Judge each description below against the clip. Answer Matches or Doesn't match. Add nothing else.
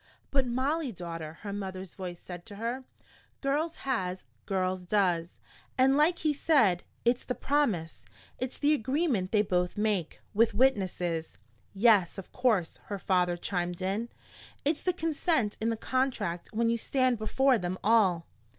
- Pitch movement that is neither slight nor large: Doesn't match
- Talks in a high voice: Matches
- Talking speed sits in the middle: Matches